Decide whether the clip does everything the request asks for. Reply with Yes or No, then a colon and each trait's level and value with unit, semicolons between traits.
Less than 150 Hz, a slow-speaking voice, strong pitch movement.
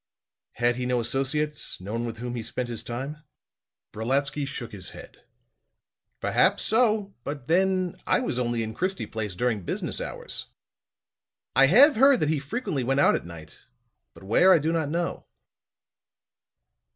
No: low, 135 Hz; average, 160 wpm; wide, 6.0 semitones